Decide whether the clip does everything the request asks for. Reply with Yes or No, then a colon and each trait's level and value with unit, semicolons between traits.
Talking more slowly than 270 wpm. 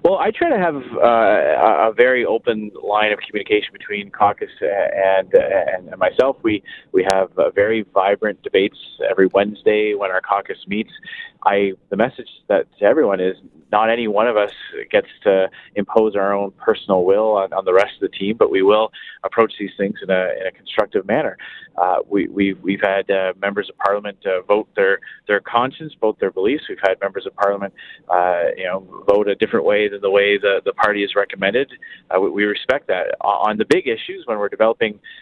Yes: average, 200 wpm